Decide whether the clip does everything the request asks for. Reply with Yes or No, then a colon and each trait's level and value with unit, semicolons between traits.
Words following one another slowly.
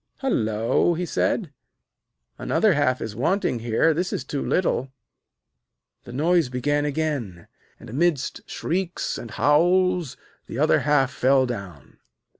Yes: slow, 125 wpm